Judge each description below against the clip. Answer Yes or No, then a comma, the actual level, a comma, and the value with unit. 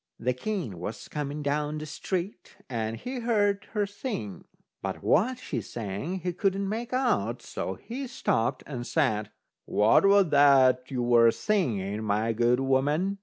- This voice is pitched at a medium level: Yes, medium, 145 Hz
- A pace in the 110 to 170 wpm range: Yes, average, 155 wpm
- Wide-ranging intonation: Yes, wide, 8.9 semitones